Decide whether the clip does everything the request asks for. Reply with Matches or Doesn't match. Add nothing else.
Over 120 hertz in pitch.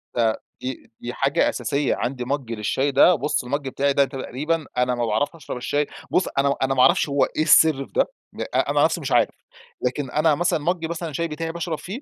Matches